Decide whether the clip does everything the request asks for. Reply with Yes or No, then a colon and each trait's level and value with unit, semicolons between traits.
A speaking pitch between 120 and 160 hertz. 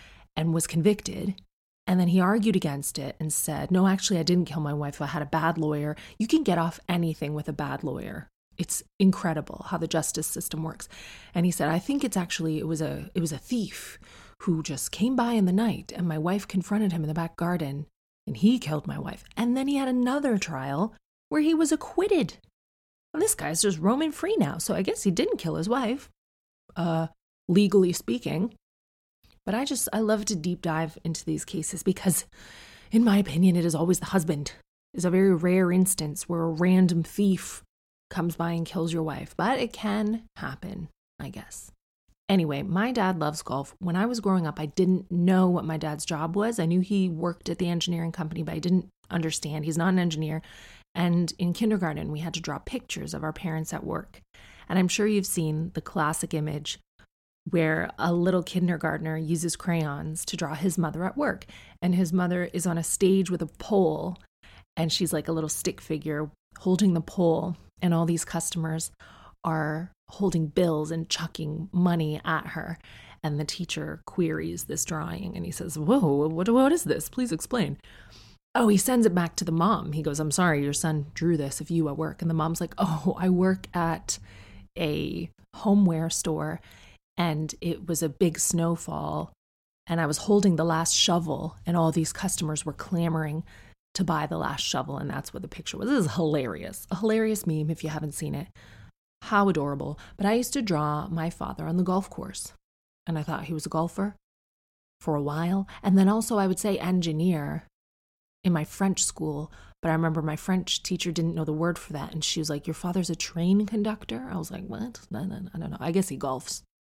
No: medium, 170 Hz